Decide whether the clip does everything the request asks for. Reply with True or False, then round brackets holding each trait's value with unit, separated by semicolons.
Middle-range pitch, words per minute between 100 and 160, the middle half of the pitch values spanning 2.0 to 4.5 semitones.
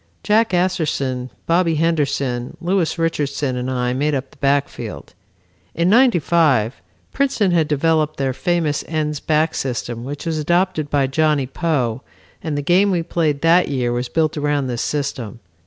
True (150 Hz; 155 wpm; 3.9 semitones)